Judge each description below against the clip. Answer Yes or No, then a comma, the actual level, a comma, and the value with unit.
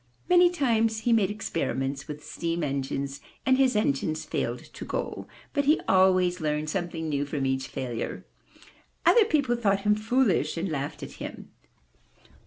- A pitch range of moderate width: No, wide, 7.7 semitones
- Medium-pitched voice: Yes, medium, 180 Hz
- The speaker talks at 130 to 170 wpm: Yes, average, 155 wpm